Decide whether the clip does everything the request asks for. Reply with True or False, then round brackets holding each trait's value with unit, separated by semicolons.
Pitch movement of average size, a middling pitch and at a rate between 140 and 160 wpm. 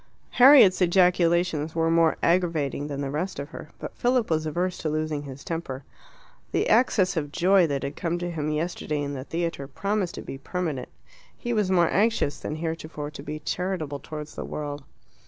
False (3.6 semitones; 165 Hz; 185 wpm)